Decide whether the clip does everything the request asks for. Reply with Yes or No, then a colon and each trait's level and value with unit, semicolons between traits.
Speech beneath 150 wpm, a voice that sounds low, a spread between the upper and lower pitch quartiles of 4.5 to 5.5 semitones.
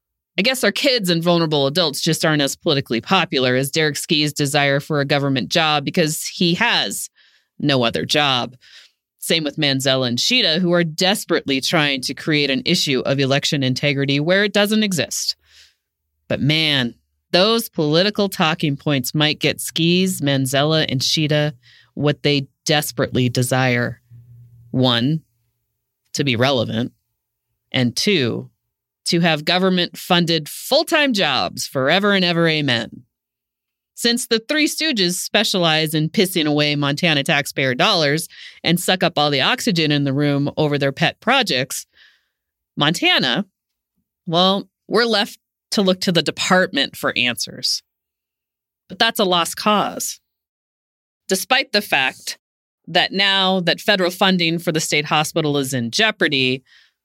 No: average, 140 wpm; medium, 155 Hz; average, 5.1 semitones